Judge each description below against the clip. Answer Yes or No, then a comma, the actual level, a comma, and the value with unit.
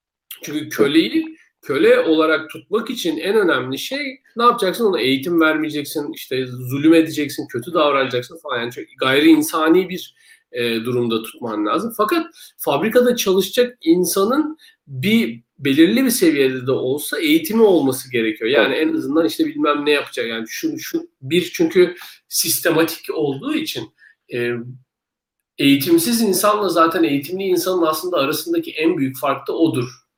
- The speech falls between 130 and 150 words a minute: Yes, average, 135 wpm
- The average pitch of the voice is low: No, medium, 175 Hz